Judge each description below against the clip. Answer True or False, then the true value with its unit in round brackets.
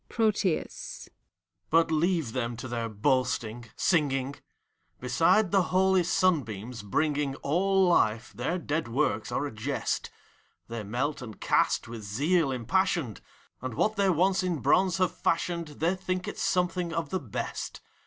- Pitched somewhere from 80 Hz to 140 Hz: False (150 Hz)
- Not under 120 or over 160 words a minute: True (145 wpm)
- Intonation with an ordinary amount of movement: False (7.1 semitones)